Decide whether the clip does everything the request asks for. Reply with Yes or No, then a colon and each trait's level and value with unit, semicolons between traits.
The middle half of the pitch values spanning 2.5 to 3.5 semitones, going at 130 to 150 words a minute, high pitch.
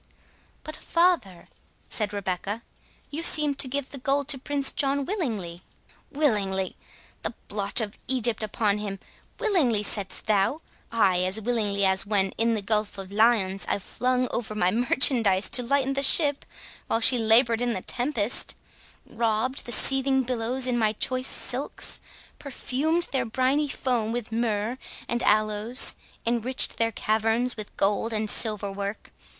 No: average, 4.0 semitones; average, 140 wpm; high, 230 Hz